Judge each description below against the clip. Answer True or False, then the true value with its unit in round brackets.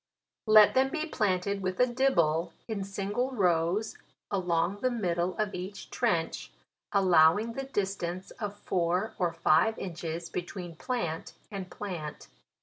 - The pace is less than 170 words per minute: True (140 wpm)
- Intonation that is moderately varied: True (3.9 semitones)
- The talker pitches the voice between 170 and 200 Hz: True (190 Hz)